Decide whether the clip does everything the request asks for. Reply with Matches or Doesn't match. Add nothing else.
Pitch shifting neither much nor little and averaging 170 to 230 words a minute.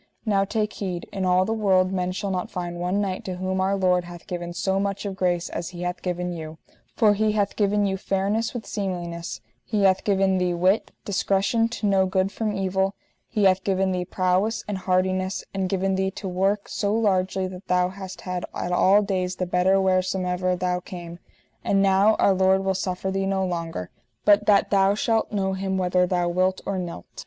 Doesn't match